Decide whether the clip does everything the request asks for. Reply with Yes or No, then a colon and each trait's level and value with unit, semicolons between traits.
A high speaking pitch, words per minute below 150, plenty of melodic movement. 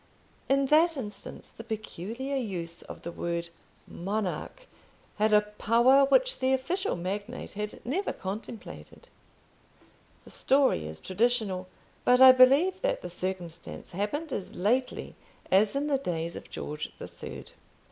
Yes: high, 220 Hz; slow, 135 wpm; wide, 6.4 semitones